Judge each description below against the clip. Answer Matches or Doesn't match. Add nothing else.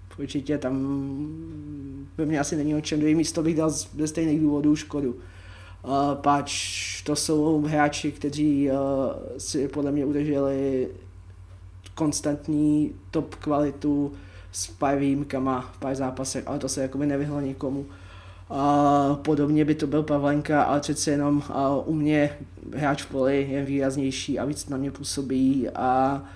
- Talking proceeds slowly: Doesn't match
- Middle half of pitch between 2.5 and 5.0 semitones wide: Doesn't match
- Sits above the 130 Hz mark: Matches